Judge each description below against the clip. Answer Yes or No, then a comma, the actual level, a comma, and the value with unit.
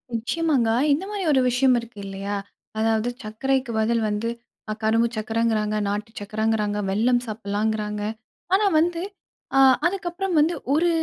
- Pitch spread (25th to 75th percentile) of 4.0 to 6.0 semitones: Yes, average, 4.7 semitones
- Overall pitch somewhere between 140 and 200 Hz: No, high, 230 Hz